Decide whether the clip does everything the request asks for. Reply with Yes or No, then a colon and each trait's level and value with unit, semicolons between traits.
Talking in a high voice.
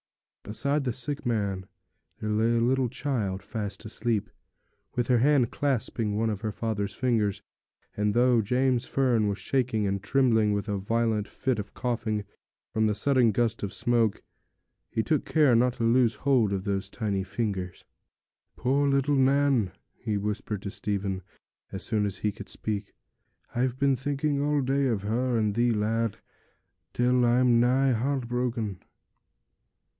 No: low, 115 Hz